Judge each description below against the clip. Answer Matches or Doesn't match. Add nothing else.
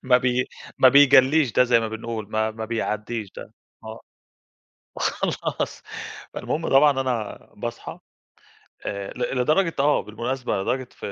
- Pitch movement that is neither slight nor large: Matches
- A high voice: Doesn't match